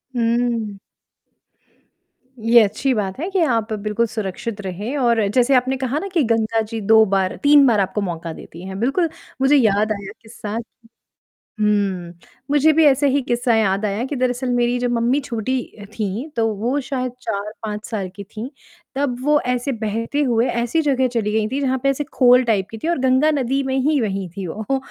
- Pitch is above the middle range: Yes, high, 235 Hz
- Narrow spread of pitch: No, average, 4.0 semitones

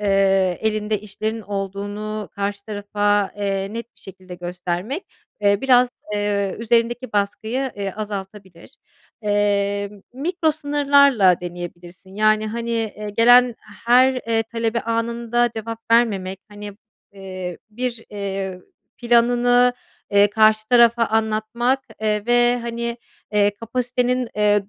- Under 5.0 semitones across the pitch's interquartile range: Yes, average, 2.9 semitones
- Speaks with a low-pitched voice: No, high, 215 Hz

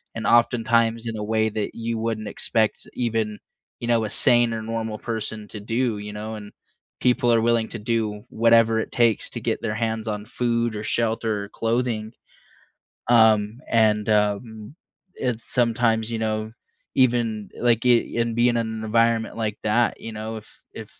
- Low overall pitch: Yes, low, 115 Hz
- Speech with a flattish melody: Yes, narrow, 1.4 semitones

